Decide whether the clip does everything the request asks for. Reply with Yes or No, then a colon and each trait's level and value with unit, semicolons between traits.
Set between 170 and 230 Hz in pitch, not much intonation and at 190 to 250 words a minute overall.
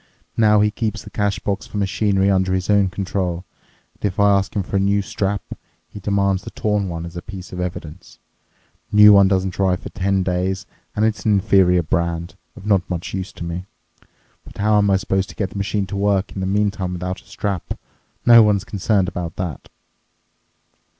No: very low, 95 Hz; narrow, 1.9 semitones; fast, 205 wpm